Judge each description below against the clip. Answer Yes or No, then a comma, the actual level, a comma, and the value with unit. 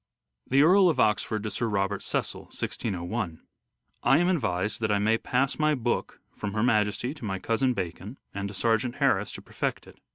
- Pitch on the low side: Yes, low, 110 Hz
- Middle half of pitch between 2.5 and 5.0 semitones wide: Yes, average, 4.1 semitones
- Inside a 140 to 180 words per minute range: No, average, 195 wpm